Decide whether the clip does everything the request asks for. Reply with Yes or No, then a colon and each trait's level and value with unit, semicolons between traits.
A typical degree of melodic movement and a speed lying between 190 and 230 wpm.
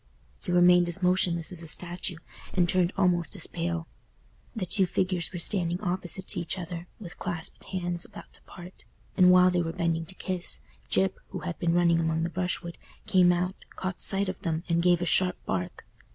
No: narrow, 1.3 semitones; average, 195 wpm